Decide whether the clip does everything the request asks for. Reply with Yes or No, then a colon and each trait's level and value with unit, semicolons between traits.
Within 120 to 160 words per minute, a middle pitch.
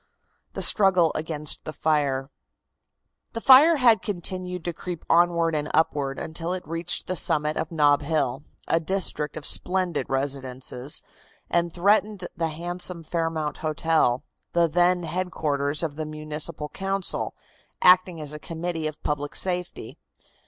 Yes: average, 140 wpm; medium, 165 Hz